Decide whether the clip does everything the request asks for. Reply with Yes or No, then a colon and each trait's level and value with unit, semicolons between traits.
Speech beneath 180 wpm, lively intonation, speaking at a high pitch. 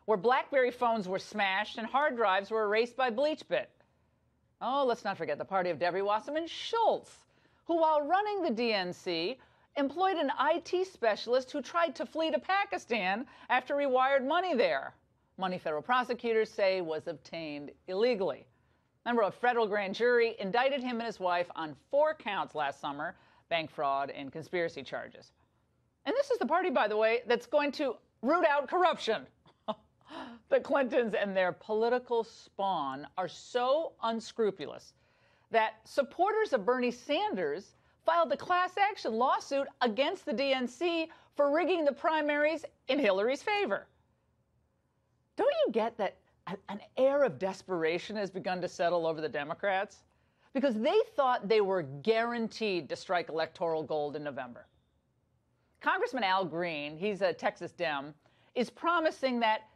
Yes: average, 150 wpm; wide, 7.4 semitones; high, 235 Hz